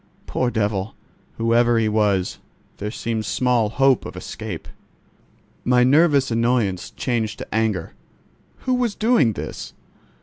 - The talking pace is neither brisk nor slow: No, slow, 125 wpm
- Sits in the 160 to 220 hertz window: No, low, 115 Hz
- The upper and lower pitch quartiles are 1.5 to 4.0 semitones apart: Yes, average, 3.0 semitones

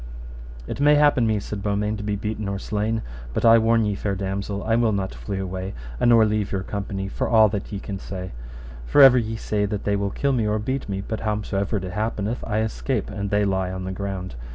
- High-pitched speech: No, low, 105 Hz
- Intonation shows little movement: Yes, narrow, 2.1 semitones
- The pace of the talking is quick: Yes, fast, 235 wpm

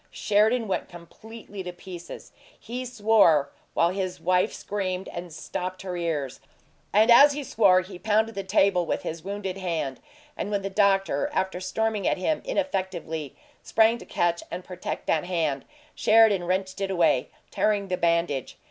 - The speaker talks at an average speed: Yes, average, 160 wpm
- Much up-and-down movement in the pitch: No, average, 3.2 semitones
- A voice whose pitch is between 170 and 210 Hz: Yes, high, 190 Hz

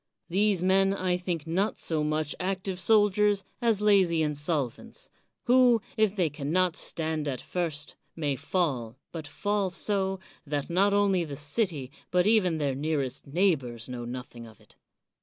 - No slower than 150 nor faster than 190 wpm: Yes, average, 155 wpm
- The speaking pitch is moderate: Yes, medium, 170 Hz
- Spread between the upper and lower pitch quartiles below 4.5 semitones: No, average, 5.0 semitones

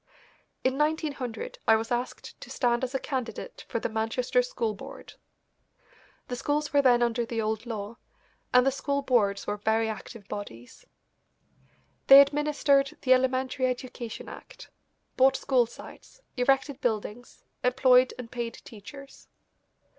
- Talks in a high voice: Yes, very high, 250 Hz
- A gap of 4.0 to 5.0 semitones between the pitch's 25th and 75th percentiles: No, average, 3.1 semitones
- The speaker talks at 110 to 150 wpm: Yes, average, 140 wpm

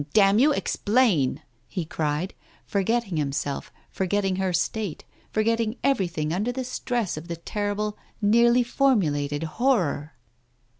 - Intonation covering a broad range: Yes, wide, 6.1 semitones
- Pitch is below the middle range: No, high, 200 Hz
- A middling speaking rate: No, slow, 130 wpm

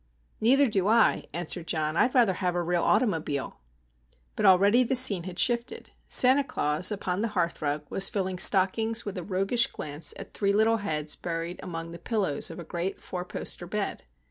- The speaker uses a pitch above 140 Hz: Yes, medium, 185 Hz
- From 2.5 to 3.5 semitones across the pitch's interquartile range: No, average, 4.5 semitones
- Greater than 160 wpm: Yes, average, 180 wpm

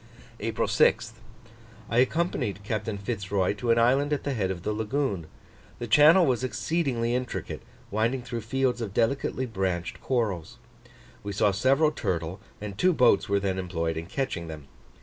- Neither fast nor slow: Yes, average, 165 wpm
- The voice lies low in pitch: Yes, low, 115 Hz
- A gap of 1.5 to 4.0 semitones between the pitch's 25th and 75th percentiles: No, average, 5.2 semitones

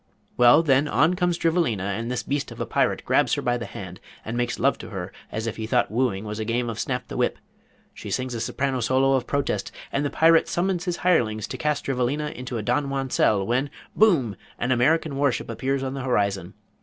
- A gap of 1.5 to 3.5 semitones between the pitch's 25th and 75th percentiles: No, average, 3.9 semitones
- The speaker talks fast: Yes, fast, 220 wpm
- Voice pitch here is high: No, low, 130 Hz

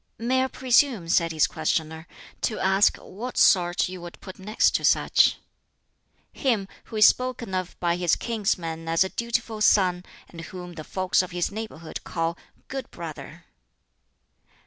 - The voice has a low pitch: No, medium, 185 Hz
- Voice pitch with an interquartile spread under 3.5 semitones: No, average, 4.6 semitones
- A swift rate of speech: No, average, 155 wpm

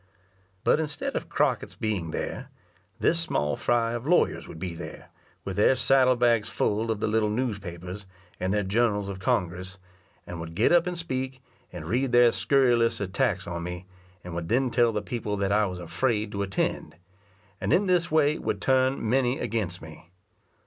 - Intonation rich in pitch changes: Yes, wide, 5.7 semitones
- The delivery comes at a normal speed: Yes, average, 180 wpm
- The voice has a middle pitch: No, low, 110 Hz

